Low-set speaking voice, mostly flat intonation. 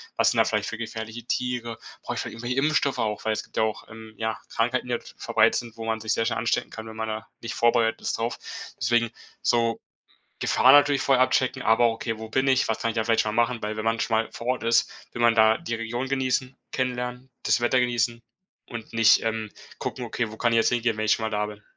Yes: low, 115 Hz; narrow, 1.8 semitones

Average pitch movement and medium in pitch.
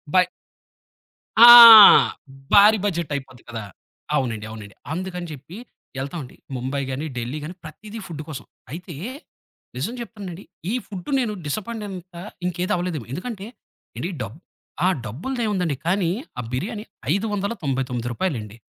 No: wide, 7.0 semitones; medium, 170 Hz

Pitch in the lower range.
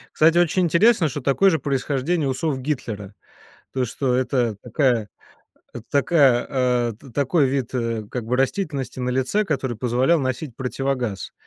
Yes: low, 130 Hz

